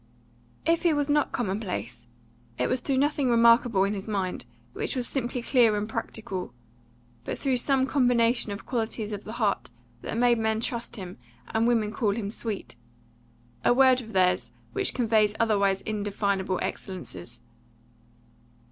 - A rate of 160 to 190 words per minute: No, average, 150 wpm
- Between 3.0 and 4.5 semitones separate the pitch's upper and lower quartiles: Yes, average, 3.6 semitones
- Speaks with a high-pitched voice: Yes, high, 225 Hz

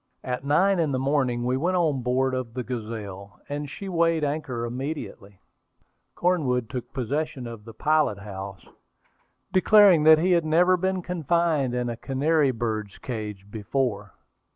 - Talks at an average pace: Yes, average, 155 wpm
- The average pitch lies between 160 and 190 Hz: No, low, 130 Hz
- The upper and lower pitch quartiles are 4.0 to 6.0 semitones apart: Yes, average, 5.3 semitones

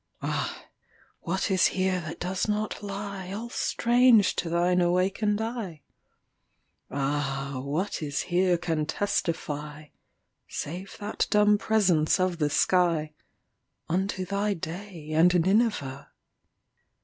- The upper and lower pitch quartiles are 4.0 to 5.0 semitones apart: Yes, average, 4.6 semitones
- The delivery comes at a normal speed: No, slow, 100 wpm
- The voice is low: No, medium, 180 Hz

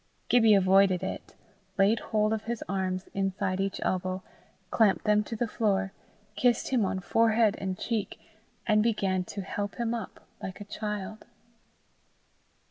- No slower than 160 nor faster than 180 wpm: No, average, 145 wpm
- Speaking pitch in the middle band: No, high, 205 Hz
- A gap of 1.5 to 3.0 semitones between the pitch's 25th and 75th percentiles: Yes, narrow, 2.5 semitones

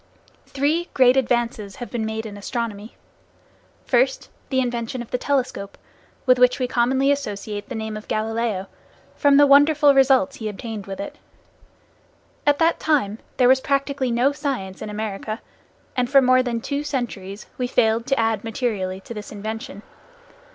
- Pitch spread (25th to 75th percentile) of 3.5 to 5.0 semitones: Yes, average, 3.9 semitones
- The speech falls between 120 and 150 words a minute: No, average, 160 wpm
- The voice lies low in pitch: No, high, 240 Hz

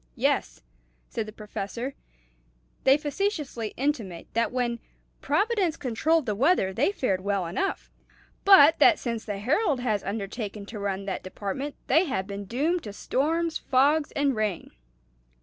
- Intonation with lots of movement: Yes, wide, 6.8 semitones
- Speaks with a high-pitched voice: Yes, high, 245 Hz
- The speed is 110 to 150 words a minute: Yes, average, 145 wpm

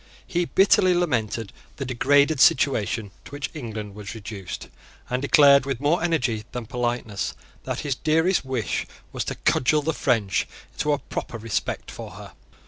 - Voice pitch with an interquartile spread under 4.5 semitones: No, average, 5.0 semitones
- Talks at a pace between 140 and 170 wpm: Yes, average, 155 wpm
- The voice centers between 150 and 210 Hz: No, low, 130 Hz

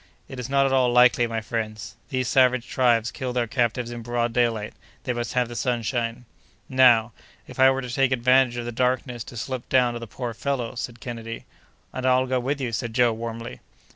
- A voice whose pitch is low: Yes, low, 120 Hz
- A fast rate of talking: Yes, fast, 210 wpm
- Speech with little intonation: Yes, narrow, 1.7 semitones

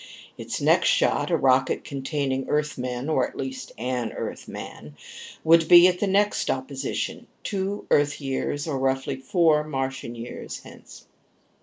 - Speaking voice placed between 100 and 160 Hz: Yes, medium, 140 Hz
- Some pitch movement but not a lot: Yes, average, 3.7 semitones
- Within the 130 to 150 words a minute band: Yes, average, 140 wpm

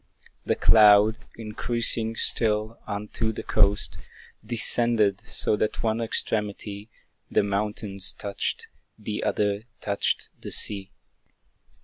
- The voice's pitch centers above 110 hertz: No, low, 105 Hz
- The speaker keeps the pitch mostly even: Yes, narrow, 1.5 semitones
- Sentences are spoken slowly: Yes, slow, 100 wpm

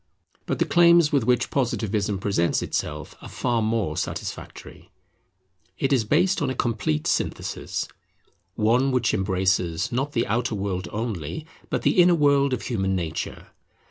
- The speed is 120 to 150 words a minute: Yes, average, 145 wpm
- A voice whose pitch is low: Yes, low, 115 Hz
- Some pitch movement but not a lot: No, wide, 5.7 semitones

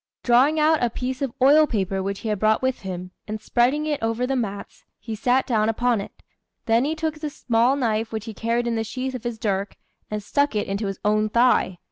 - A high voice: Yes, high, 230 Hz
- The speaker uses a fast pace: Yes, fast, 230 wpm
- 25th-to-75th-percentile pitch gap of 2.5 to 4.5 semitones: Yes, average, 3.5 semitones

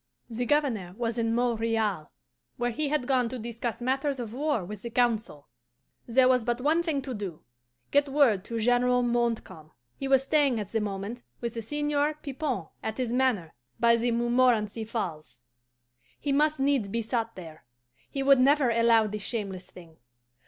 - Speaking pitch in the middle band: No, high, 235 Hz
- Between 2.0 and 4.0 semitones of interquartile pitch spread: Yes, average, 3.6 semitones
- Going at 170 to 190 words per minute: Yes, average, 175 wpm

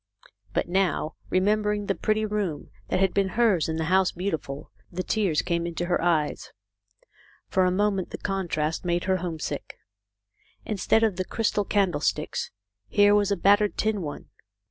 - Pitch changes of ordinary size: Yes, average, 3.1 semitones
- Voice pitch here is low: No, high, 190 Hz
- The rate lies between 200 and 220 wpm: No, average, 165 wpm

